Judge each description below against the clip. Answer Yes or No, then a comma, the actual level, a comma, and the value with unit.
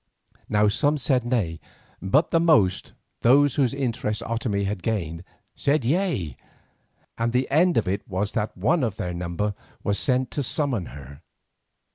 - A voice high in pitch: No, low, 115 Hz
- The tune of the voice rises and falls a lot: Yes, wide, 6.3 semitones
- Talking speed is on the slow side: No, average, 155 wpm